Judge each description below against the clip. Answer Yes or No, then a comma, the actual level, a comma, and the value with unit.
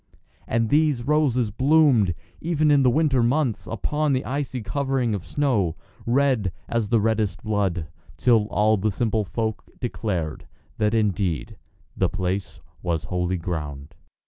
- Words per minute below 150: Yes, average, 140 wpm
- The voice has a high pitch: No, low, 110 Hz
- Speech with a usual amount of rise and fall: No, wide, 5.8 semitones